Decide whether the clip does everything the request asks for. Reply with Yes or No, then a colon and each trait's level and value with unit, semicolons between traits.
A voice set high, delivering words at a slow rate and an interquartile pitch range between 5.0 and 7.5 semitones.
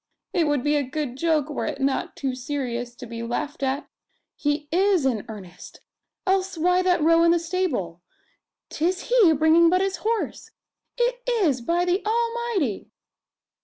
No: very high, 315 Hz; average, 165 wpm; wide, 5.6 semitones